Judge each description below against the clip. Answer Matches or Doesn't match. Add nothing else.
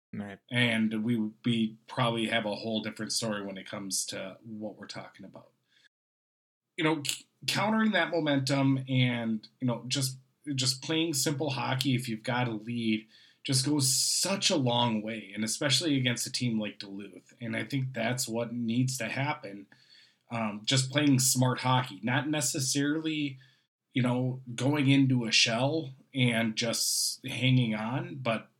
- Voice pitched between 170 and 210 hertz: Doesn't match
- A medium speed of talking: Matches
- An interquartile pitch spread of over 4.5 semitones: Doesn't match